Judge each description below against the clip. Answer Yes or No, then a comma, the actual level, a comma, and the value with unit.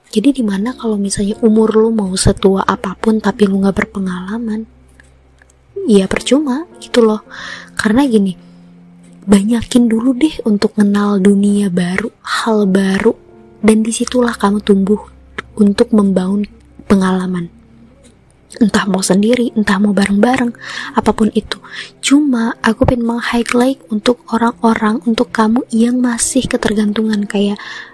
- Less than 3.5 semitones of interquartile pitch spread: Yes, average, 2.8 semitones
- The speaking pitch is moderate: No, high, 215 Hz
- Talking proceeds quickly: No, average, 120 wpm